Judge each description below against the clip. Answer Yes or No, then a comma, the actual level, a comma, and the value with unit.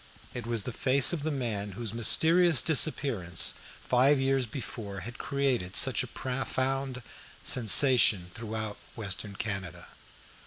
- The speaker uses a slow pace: Yes, slow, 125 wpm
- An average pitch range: Yes, average, 4.4 semitones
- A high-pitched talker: No, low, 120 Hz